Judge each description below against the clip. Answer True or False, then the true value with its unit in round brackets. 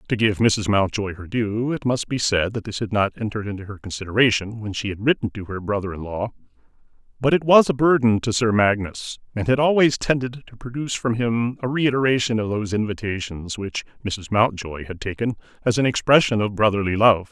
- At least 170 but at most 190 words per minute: False (205 wpm)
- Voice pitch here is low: True (110 Hz)